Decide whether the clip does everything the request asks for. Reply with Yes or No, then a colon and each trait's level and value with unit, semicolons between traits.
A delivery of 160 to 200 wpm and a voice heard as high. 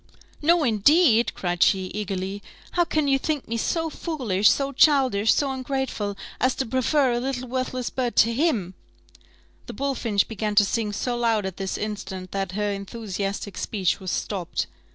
Yes: average, 170 wpm; high, 230 Hz